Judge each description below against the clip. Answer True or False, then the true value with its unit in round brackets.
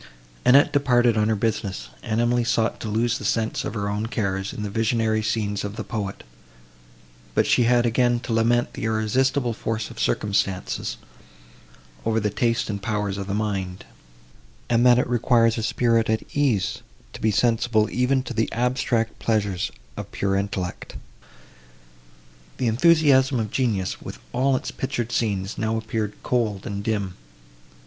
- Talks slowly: False (160 wpm)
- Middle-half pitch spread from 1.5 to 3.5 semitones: True (2.6 semitones)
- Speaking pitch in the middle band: False (110 Hz)